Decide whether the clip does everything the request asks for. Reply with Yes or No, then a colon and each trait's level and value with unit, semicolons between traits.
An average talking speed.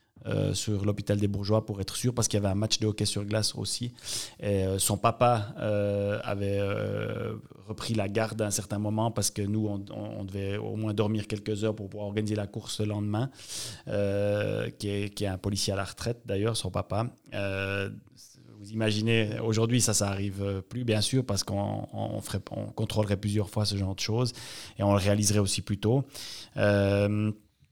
Yes: average, 205 wpm